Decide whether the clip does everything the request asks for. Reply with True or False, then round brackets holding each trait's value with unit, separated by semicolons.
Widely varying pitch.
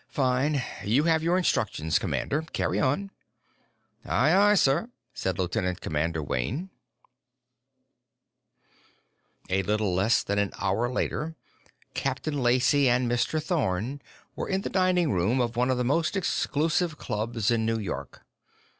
True (7.4 semitones)